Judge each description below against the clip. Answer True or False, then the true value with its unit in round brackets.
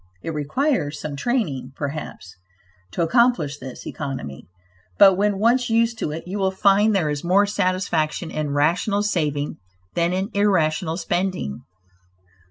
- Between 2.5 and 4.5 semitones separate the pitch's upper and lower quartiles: False (5.3 semitones)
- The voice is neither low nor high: True (175 Hz)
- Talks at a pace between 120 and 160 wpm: True (140 wpm)